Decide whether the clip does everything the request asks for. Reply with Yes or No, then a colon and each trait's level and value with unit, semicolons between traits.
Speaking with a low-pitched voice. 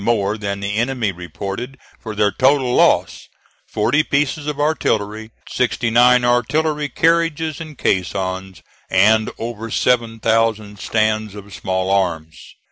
Yes: low, 110 Hz